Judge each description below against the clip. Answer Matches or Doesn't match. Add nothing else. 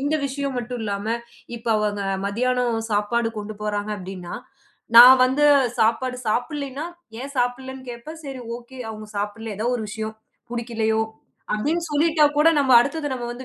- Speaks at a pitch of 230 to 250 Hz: Matches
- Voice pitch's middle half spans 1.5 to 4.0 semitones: Matches